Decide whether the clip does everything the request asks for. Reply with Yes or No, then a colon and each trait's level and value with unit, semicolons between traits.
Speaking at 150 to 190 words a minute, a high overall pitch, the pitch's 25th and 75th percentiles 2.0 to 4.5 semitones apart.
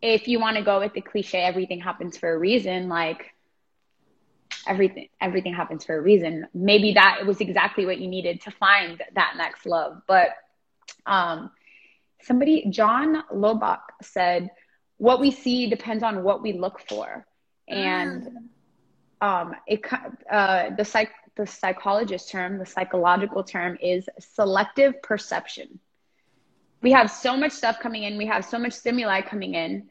Yes: average, 155 wpm; high, 205 Hz; average, 3.6 semitones